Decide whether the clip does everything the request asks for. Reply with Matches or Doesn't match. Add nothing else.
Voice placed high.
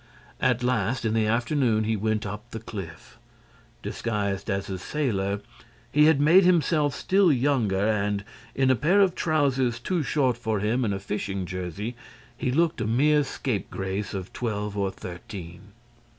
Doesn't match